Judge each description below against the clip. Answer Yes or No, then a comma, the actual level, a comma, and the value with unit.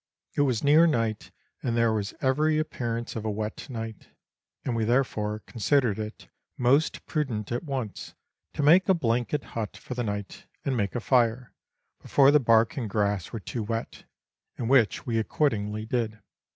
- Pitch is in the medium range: No, low, 115 Hz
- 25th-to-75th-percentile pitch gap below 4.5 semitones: Yes, average, 3.8 semitones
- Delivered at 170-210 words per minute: Yes, average, 175 wpm